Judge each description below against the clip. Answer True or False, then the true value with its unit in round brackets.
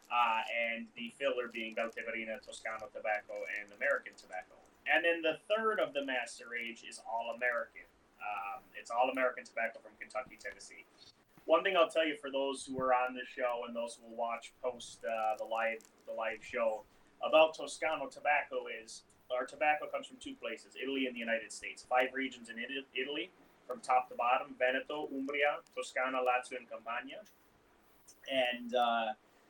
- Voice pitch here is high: False (125 Hz)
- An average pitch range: True (3.5 semitones)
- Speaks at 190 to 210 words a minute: False (175 wpm)